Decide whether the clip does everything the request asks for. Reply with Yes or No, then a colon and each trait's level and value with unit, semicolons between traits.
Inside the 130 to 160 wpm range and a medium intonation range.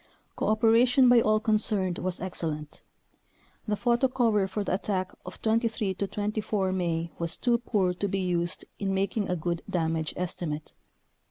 Yes: average, 150 wpm; average, 3.5 semitones